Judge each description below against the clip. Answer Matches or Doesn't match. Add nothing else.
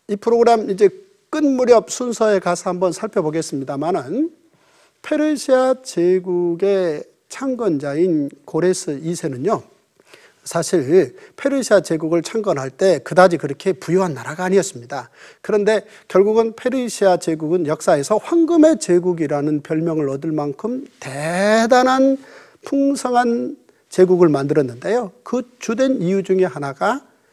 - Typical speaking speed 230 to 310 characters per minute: Matches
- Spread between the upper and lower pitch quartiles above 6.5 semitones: Matches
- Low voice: Doesn't match